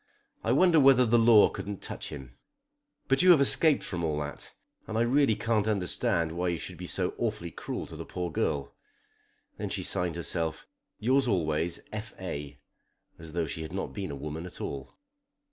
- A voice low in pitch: Yes, very low, 90 Hz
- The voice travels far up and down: Yes, wide, 6.7 semitones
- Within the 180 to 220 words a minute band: Yes, average, 190 wpm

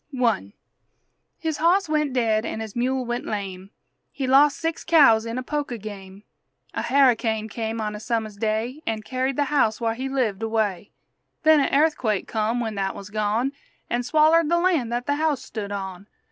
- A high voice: Yes, high, 235 Hz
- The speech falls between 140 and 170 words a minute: No, average, 185 wpm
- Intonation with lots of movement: No, average, 4.6 semitones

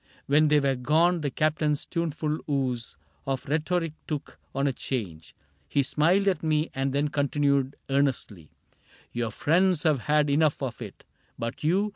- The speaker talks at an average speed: Yes, average, 160 wpm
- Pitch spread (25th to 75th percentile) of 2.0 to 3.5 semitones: Yes, narrow, 2.6 semitones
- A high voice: No, medium, 145 Hz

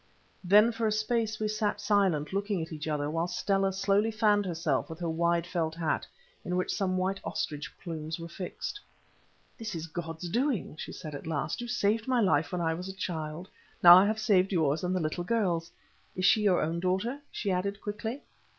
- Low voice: No, medium, 185 Hz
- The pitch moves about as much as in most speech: Yes, average, 4.2 semitones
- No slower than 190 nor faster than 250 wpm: Yes, fast, 205 wpm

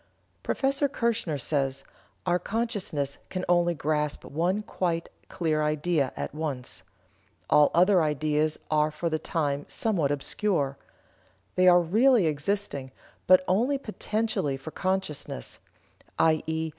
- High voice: No, medium, 160 Hz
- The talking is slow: Yes, slow, 120 wpm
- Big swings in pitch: No, average, 4.2 semitones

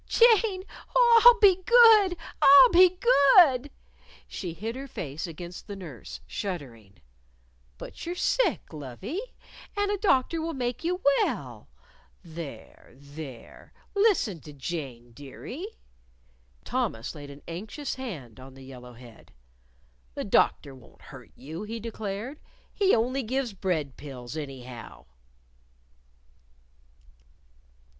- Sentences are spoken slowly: Yes, slow, 120 wpm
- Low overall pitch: No, high, 200 Hz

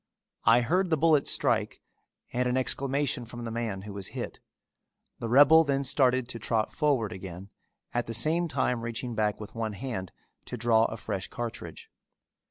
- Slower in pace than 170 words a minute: No, average, 175 wpm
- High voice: No, low, 120 Hz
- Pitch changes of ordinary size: Yes, average, 3.8 semitones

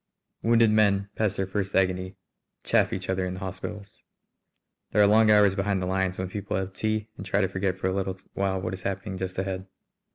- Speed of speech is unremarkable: No, fast, 215 wpm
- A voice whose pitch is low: Yes, very low, 95 Hz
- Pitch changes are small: Yes, narrow, 1.5 semitones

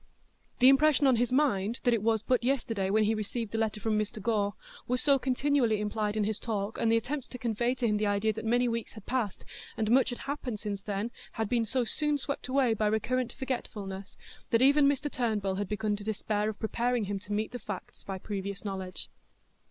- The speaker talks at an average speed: No, fast, 220 wpm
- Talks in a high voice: Yes, high, 225 Hz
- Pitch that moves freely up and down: No, average, 3.2 semitones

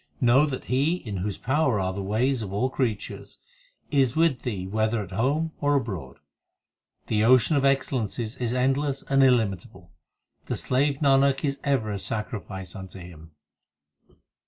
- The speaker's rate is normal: Yes, average, 155 wpm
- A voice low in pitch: Yes, low, 125 Hz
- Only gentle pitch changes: No, average, 5.1 semitones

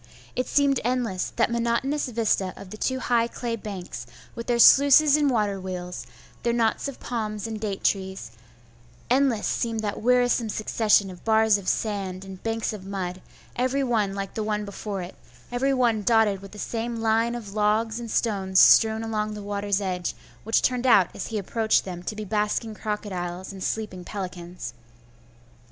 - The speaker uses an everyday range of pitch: Yes, average, 3.2 semitones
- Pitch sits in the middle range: No, high, 215 Hz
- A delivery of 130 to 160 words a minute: No, average, 175 wpm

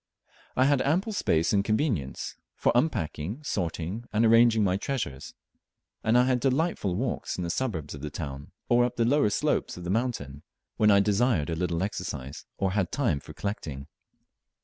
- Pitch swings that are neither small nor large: No, wide, 6.9 semitones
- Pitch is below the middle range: Yes, low, 105 Hz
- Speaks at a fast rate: No, average, 175 wpm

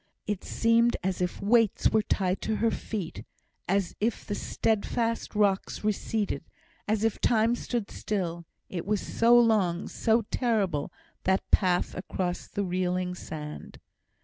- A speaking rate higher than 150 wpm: No, average, 140 wpm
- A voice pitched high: Yes, high, 205 Hz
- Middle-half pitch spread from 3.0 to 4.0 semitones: Yes, average, 3.6 semitones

